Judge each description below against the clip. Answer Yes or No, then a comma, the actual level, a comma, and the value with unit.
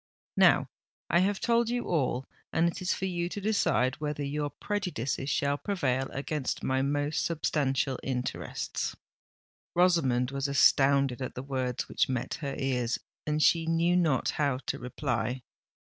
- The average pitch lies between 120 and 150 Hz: Yes, medium, 140 Hz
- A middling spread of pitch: Yes, average, 4.4 semitones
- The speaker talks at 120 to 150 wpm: Yes, average, 145 wpm